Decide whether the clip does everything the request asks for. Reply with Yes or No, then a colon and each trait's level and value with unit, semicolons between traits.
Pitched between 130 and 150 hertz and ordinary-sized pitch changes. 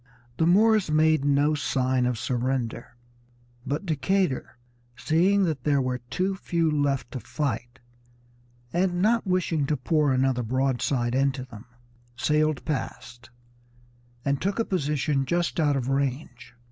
Yes: medium, 140 Hz; average, 4.1 semitones